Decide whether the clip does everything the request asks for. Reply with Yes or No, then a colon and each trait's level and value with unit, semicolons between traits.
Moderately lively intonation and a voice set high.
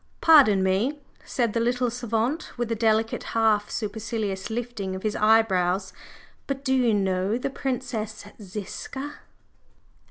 Yes: average, 3.1 semitones; high, 225 Hz